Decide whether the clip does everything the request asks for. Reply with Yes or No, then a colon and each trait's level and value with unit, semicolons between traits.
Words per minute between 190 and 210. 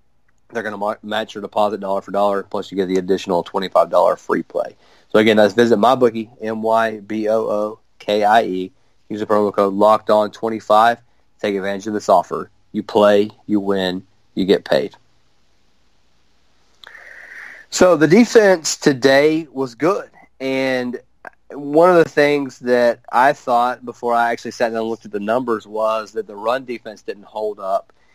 No: average, 155 wpm